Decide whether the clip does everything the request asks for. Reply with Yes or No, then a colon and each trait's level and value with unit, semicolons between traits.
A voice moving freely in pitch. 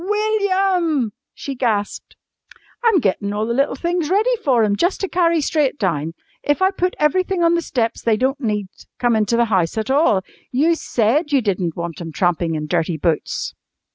Yes: wide, 8.9 semitones